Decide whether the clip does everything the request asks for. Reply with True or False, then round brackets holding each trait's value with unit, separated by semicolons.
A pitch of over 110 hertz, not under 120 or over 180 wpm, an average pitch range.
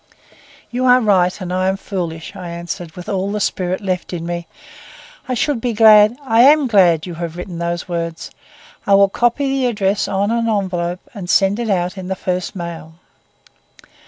False (190 Hz; 190 wpm; 3.9 semitones)